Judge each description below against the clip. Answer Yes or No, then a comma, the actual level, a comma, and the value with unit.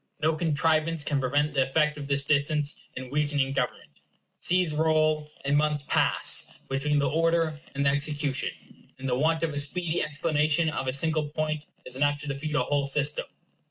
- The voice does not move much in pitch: Yes, narrow, 1.9 semitones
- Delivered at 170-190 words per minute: Yes, average, 180 wpm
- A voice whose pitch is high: No, medium, 150 Hz